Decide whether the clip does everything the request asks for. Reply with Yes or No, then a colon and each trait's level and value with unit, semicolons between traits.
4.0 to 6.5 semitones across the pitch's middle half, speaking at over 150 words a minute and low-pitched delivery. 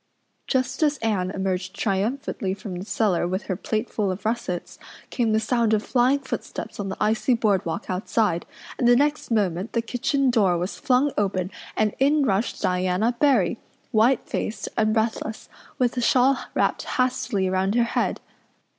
No: average, 4.5 semitones; average, 165 wpm; high, 220 Hz